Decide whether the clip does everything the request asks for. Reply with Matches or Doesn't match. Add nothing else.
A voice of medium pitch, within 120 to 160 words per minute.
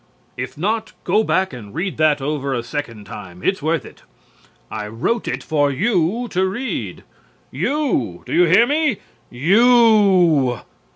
Matches